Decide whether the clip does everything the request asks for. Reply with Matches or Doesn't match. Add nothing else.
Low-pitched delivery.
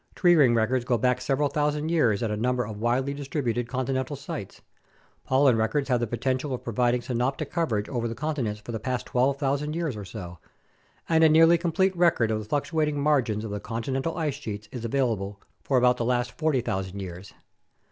Matches